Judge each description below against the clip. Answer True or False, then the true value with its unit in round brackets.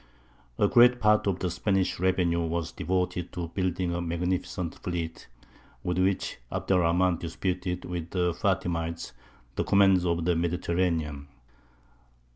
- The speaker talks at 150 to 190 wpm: False (135 wpm)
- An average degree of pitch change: False (1.7 semitones)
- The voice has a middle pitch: False (90 Hz)